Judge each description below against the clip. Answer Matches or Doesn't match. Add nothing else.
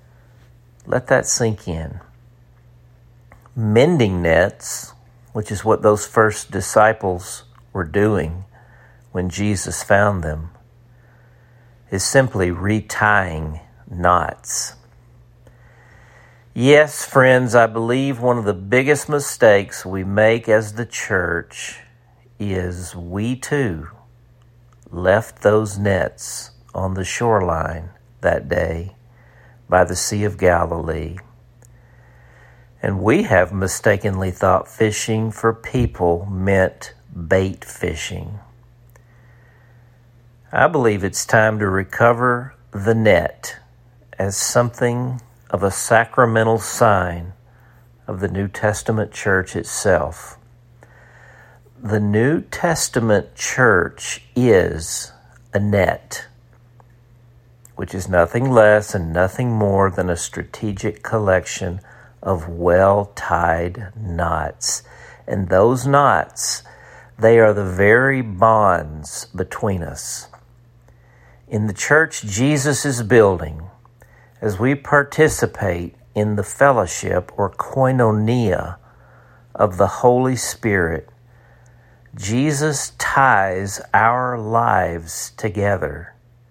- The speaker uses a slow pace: Matches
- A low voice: Matches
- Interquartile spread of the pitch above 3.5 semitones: Matches